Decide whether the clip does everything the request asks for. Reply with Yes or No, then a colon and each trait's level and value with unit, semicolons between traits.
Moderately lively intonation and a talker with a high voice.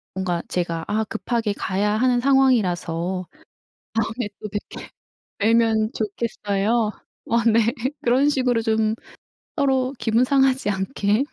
Yes: average, 3.4 semitones; high, 220 Hz